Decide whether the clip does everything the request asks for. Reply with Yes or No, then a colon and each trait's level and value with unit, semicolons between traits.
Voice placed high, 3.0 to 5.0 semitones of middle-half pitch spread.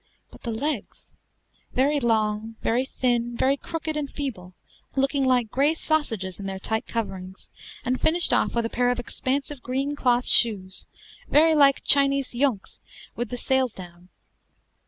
Yes: very high, 250 Hz; average, 3.9 semitones